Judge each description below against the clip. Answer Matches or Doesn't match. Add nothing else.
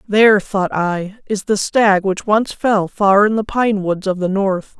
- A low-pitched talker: Doesn't match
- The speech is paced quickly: Matches